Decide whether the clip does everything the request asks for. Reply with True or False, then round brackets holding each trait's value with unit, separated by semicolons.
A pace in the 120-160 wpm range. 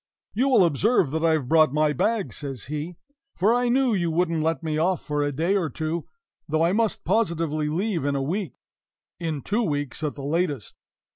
False (205 wpm)